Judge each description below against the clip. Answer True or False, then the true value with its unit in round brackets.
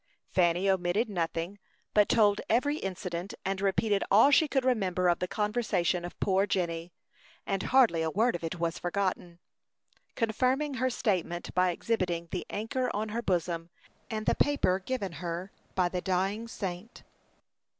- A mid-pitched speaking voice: False (195 Hz)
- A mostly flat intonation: False (4.0 semitones)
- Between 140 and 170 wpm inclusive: True (155 wpm)